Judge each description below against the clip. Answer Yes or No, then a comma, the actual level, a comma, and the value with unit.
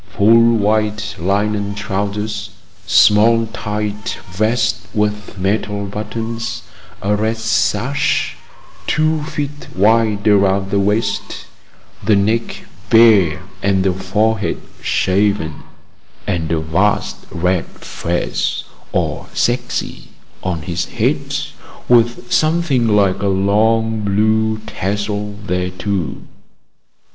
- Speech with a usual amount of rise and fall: No, narrow, 2.2 semitones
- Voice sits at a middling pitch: No, low, 105 Hz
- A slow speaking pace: Yes, slow, 95 wpm